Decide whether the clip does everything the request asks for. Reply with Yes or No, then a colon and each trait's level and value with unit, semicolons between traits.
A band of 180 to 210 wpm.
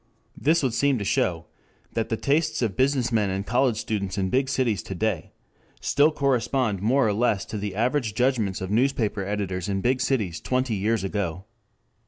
Yes: average, 185 wpm